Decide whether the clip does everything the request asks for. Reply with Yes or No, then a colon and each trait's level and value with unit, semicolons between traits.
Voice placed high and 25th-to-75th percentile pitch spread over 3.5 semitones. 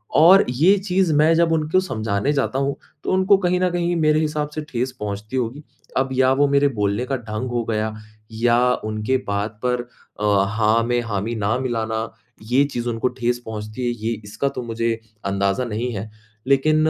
No: low, 120 Hz; average, 5.3 semitones